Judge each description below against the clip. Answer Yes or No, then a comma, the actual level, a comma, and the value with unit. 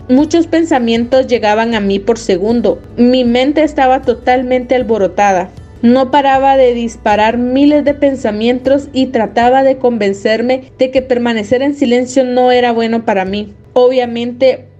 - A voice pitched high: Yes, very high, 250 Hz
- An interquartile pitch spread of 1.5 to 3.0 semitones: Yes, narrow, 2.5 semitones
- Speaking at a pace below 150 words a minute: Yes, average, 140 wpm